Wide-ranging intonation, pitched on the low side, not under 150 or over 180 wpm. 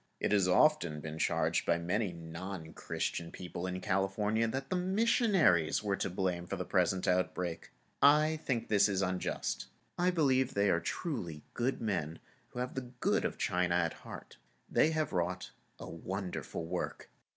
Yes: wide, 7.0 semitones; very low, 95 Hz; average, 165 wpm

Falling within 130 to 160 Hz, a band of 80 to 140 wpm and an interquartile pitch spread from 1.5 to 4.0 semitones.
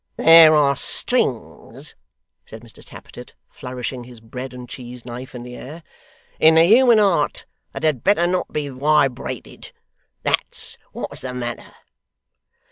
No: low, 135 Hz; slow, 135 wpm; average, 4.6 semitones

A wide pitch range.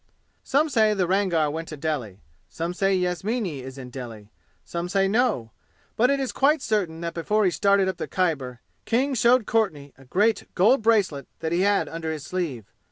Yes: wide, 5.9 semitones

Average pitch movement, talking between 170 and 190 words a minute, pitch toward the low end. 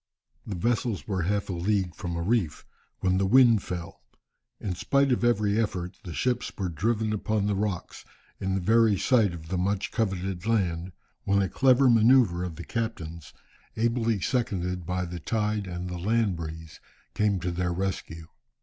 Yes: average, 4.0 semitones; average, 175 wpm; very low, 95 Hz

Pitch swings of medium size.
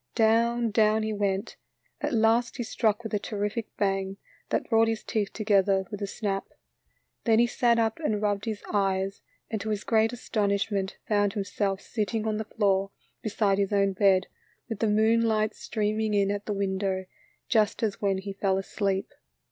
No: narrow, 2.0 semitones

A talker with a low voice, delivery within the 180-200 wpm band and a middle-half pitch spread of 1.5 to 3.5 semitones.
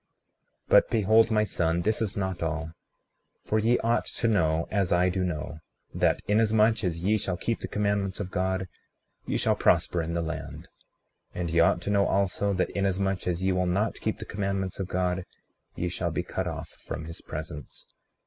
Yes: very low, 95 Hz; average, 195 wpm; average, 3.1 semitones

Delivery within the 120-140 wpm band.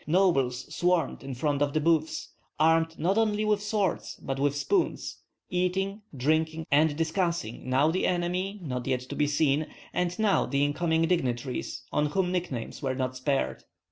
No: average, 165 wpm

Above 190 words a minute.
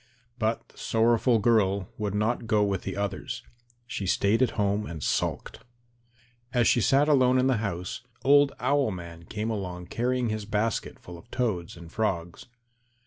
No: average, 165 wpm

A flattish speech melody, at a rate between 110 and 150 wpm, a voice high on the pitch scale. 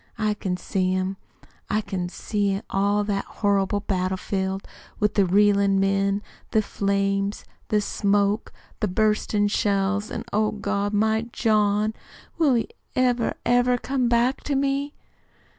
Yes: narrow, 1.8 semitones; average, 140 wpm; high, 205 Hz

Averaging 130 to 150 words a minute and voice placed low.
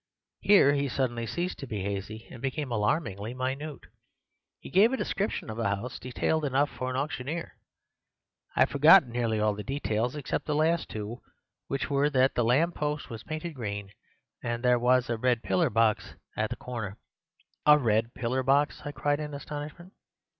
No: average, 180 wpm; low, 130 Hz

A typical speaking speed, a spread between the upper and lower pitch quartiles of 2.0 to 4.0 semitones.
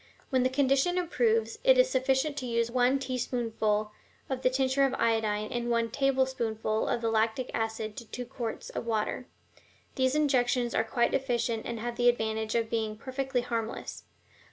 Yes: average, 170 wpm; average, 2.8 semitones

